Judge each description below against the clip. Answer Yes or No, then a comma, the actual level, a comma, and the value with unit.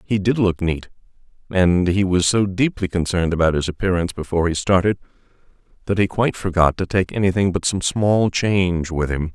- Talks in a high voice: No, very low, 95 Hz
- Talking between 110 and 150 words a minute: No, average, 185 wpm